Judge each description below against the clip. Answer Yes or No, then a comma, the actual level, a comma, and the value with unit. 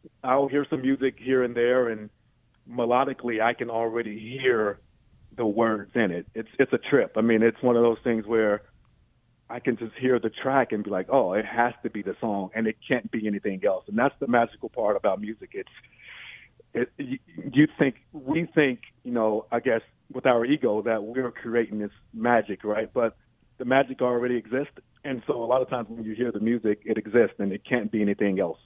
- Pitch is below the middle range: Yes, low, 115 Hz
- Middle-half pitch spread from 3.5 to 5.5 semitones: No, average, 2.7 semitones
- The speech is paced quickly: Yes, fast, 210 wpm